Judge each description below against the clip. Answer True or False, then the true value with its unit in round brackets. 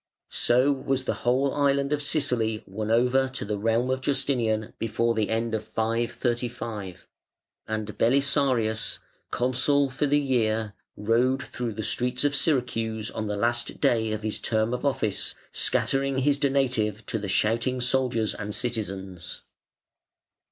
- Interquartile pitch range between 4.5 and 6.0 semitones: False (3.3 semitones)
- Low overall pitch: True (120 Hz)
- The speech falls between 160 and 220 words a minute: False (145 wpm)